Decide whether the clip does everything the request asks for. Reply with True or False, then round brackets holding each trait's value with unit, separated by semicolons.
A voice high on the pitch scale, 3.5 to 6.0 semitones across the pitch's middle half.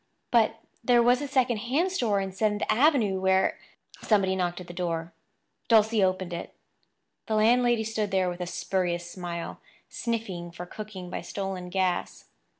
True (195 Hz; 4.1 semitones)